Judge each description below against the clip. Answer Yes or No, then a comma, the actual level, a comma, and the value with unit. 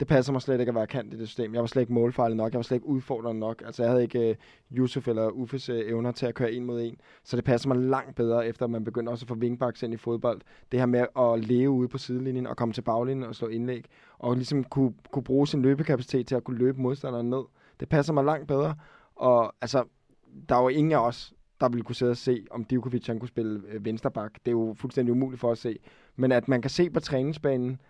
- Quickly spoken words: Yes, fast, 265 wpm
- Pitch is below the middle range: Yes, low, 125 Hz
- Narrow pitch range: Yes, narrow, 1.9 semitones